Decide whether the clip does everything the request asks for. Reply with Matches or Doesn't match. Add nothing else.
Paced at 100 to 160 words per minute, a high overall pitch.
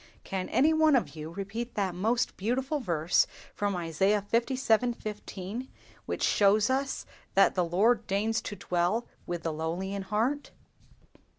Matches